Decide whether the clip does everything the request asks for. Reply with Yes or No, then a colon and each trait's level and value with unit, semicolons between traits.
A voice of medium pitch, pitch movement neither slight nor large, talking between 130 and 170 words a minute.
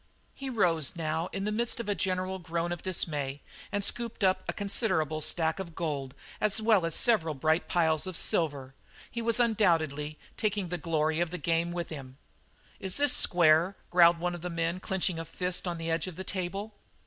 No: medium, 175 Hz; average, 3.3 semitones; average, 195 wpm